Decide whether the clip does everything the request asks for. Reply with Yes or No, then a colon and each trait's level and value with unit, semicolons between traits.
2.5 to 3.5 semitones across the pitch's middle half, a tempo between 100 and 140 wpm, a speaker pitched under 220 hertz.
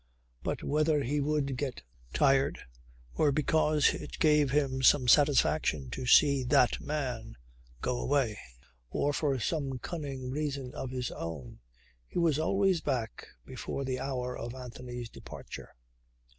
Yes: average, 2.9 semitones; slow, 135 wpm; low, 135 Hz